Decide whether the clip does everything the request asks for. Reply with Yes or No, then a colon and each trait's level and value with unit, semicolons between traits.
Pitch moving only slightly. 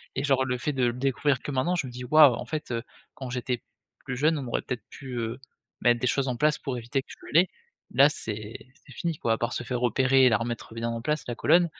No: average, 3.0 semitones